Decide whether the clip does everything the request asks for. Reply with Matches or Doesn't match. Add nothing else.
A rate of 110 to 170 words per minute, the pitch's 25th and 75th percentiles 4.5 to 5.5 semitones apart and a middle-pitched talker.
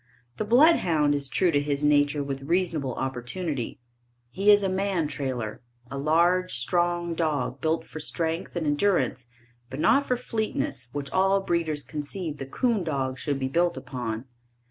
Matches